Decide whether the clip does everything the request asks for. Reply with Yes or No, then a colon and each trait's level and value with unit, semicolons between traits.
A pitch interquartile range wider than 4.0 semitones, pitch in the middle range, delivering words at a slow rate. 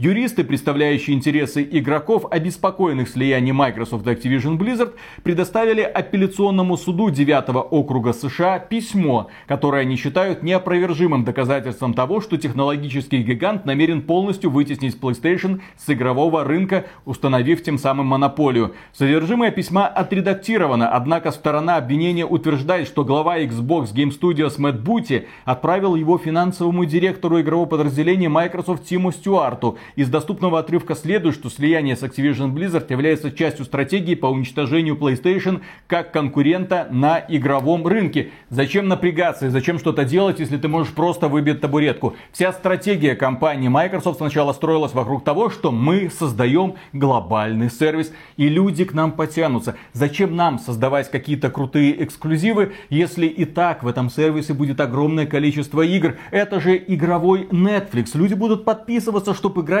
No: average, 4.5 semitones; medium, 155 Hz; average, 135 wpm